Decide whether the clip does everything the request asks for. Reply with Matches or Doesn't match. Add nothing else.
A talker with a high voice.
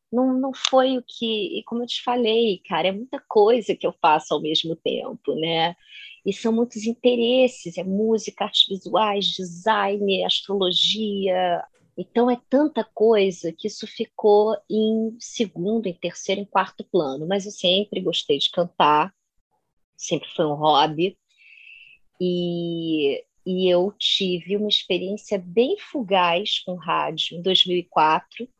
Matches